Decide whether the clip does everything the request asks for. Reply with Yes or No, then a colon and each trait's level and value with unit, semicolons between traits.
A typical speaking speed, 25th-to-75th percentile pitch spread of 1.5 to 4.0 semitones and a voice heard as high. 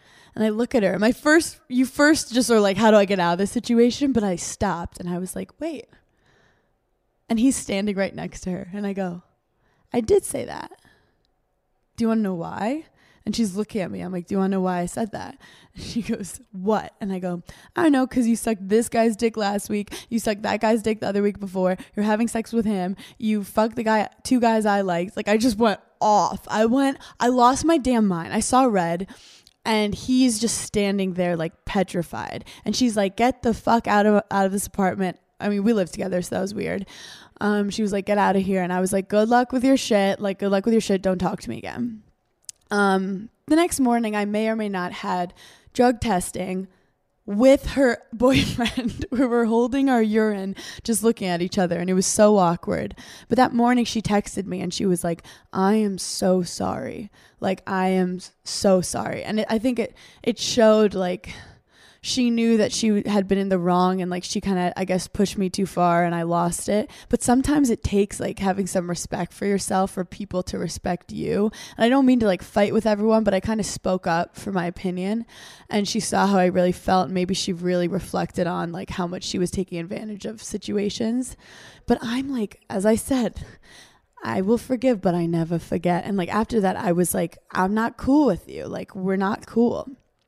No: fast, 225 wpm; average, 3.7 semitones; high, 205 Hz